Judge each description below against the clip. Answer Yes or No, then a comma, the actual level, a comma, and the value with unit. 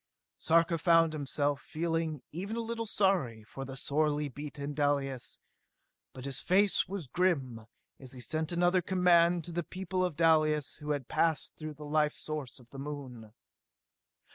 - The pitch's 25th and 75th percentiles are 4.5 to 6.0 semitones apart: No, average, 3.6 semitones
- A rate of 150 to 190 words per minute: Yes, average, 155 wpm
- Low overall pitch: No, medium, 155 Hz